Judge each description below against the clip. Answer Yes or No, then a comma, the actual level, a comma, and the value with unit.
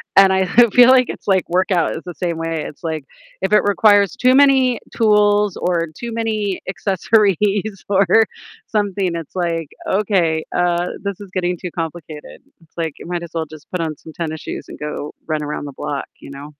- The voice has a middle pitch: Yes, medium, 180 Hz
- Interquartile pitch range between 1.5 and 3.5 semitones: No, average, 3.9 semitones